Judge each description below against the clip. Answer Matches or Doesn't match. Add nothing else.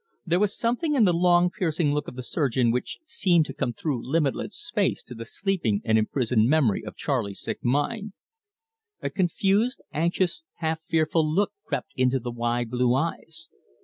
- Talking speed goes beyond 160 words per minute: Matches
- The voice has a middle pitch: Matches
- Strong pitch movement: Matches